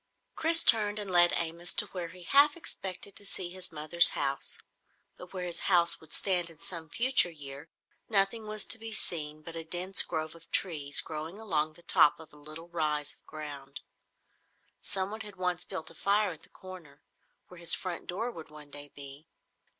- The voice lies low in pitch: No, medium, 170 Hz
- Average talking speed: Yes, average, 190 wpm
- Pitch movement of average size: Yes, average, 3.9 semitones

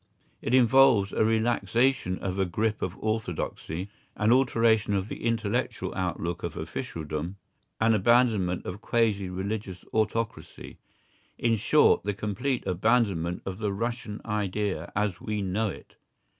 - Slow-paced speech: Yes, slow, 130 wpm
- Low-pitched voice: Yes, low, 105 Hz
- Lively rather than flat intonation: No, average, 3.5 semitones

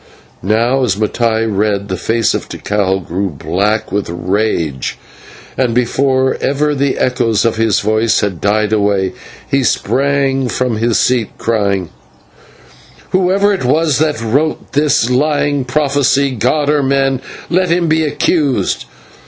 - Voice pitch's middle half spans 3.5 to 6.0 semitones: Yes, average, 5.2 semitones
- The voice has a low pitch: Yes, low, 120 Hz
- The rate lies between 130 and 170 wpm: Yes, slow, 135 wpm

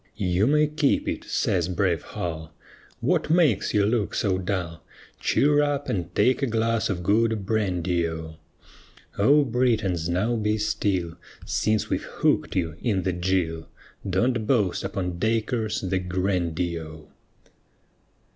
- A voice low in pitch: Yes, low, 100 Hz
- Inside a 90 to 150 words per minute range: Yes, slow, 135 wpm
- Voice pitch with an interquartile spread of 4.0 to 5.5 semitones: Yes, average, 4.4 semitones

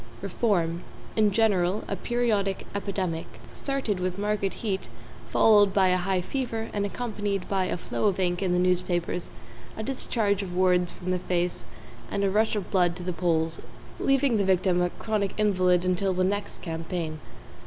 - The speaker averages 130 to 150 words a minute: No, average, 170 wpm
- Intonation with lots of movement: No, narrow, 2.6 semitones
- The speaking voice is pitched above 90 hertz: Yes, high, 190 Hz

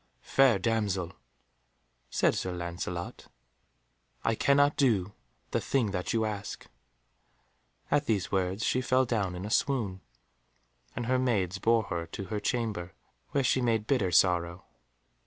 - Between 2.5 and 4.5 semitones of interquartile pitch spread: No, average, 4.9 semitones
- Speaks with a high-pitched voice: No, low, 105 Hz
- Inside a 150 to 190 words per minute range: No, average, 140 wpm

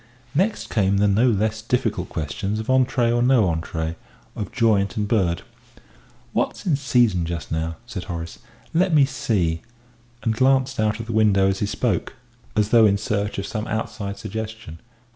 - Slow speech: No, average, 170 wpm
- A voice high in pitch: No, low, 110 Hz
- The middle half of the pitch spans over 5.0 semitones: No, average, 3.6 semitones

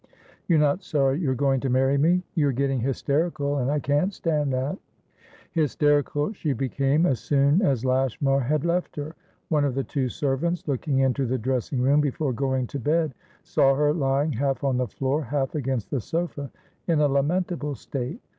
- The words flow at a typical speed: Yes, average, 180 wpm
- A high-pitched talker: No, medium, 140 Hz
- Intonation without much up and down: Yes, narrow, 2.2 semitones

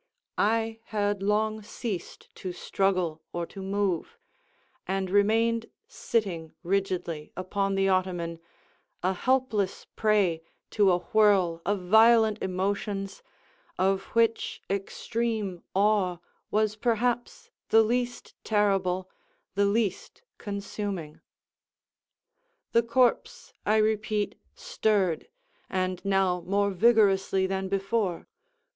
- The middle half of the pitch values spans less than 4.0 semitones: Yes, average, 2.7 semitones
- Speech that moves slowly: Yes, slow, 100 wpm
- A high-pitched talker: Yes, high, 200 Hz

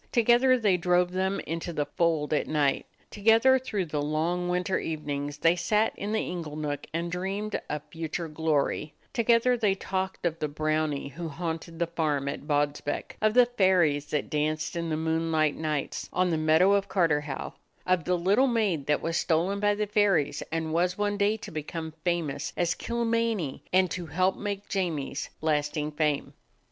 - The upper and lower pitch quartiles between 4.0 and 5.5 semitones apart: Yes, average, 4.4 semitones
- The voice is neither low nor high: Yes, medium, 170 Hz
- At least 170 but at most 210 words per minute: Yes, average, 175 wpm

